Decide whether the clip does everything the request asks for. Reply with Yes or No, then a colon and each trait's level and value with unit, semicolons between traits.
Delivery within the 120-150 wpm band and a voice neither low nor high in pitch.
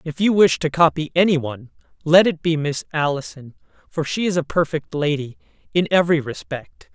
No: average, 180 wpm; medium, 160 Hz